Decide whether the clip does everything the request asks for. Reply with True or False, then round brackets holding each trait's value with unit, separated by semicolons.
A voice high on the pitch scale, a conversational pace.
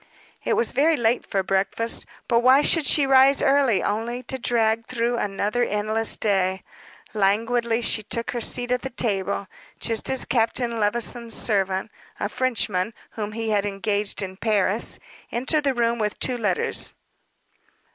True (230 Hz; 155 wpm)